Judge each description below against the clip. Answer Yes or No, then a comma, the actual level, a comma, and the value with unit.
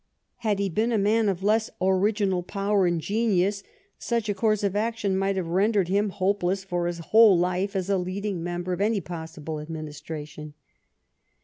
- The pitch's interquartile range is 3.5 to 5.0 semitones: No, average, 2.9 semitones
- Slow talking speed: No, average, 175 wpm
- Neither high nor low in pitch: No, high, 195 Hz